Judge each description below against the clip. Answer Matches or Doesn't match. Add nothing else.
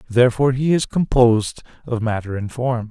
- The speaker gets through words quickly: Doesn't match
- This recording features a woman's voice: Doesn't match